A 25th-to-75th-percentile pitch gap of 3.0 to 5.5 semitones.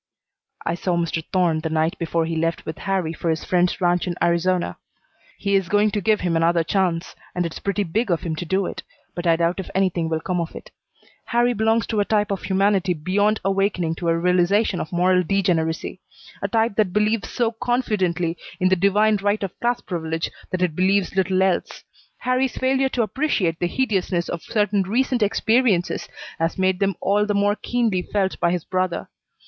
Yes: average, 3.3 semitones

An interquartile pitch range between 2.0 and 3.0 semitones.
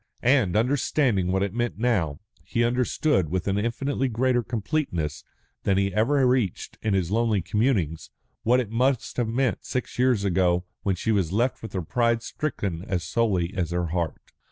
No: average, 5.1 semitones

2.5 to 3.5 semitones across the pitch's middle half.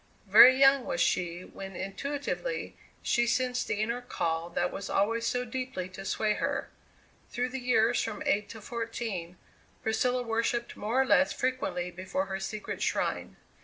No: average, 4.7 semitones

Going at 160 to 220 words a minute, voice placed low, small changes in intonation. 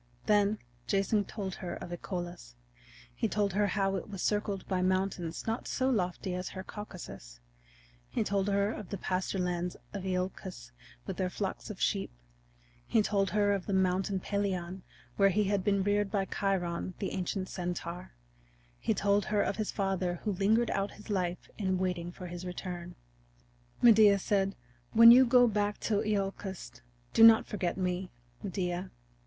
No: average, 165 wpm; high, 195 Hz; narrow, 2.2 semitones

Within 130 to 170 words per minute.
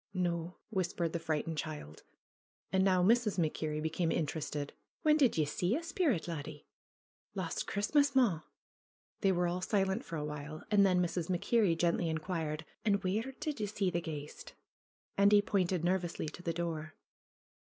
Yes: average, 165 wpm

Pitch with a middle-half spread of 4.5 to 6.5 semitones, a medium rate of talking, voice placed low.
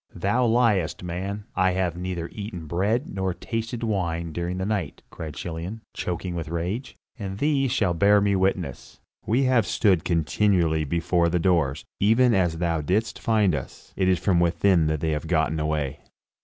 No: average, 3.8 semitones; average, 170 wpm; very low, 90 Hz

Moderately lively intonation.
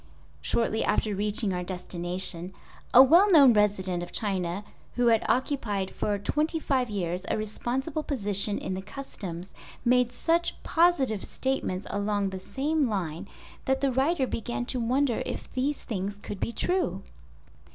No: wide, 5.7 semitones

